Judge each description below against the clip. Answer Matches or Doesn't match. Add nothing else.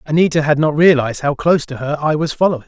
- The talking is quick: Matches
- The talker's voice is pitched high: Doesn't match